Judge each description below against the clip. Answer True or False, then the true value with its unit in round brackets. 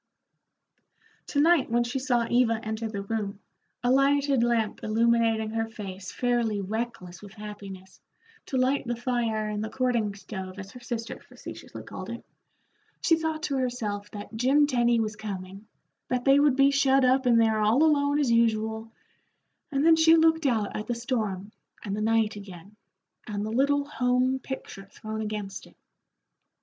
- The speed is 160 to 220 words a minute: True (165 wpm)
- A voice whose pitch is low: False (230 Hz)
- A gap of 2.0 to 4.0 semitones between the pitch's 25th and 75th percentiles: True (3.7 semitones)